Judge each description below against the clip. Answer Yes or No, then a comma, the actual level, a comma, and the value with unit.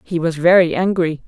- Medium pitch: Yes, medium, 170 Hz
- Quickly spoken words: No, average, 190 wpm